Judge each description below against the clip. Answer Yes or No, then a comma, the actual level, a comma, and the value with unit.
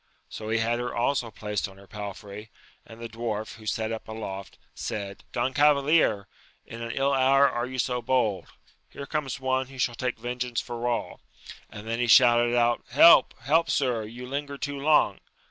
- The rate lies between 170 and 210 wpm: Yes, average, 185 wpm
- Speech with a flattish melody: No, average, 3.0 semitones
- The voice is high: No, low, 120 Hz